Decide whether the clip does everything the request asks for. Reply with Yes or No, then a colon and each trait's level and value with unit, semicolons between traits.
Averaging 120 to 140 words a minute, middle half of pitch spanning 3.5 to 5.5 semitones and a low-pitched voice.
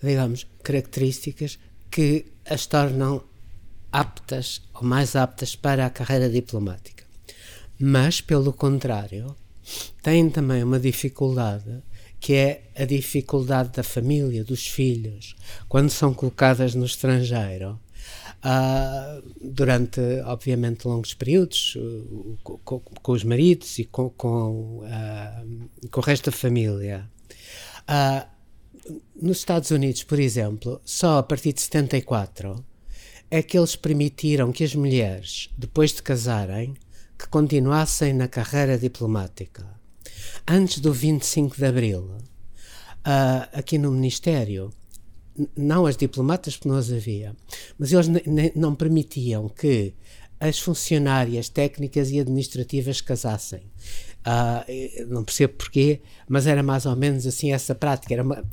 Yes: average, 125 wpm; average, 4.4 semitones; low, 130 Hz